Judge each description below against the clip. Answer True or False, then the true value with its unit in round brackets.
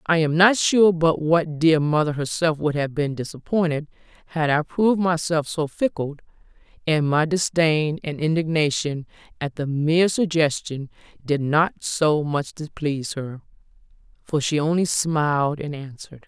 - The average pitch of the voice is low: False (155 Hz)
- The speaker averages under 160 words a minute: True (145 wpm)